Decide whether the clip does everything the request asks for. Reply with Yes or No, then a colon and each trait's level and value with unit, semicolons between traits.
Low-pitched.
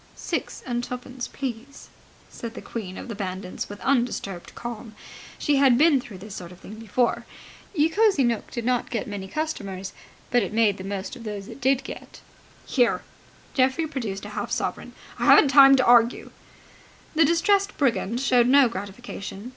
No: high, 240 Hz